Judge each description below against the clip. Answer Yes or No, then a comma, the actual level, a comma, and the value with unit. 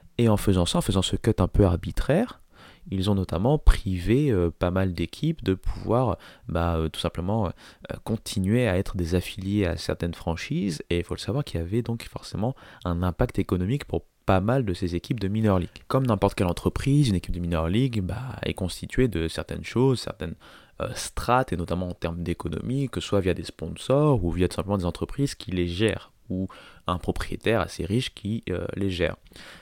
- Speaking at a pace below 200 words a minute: No, average, 210 wpm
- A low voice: Yes, very low, 95 Hz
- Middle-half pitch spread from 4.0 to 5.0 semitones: Yes, average, 4.7 semitones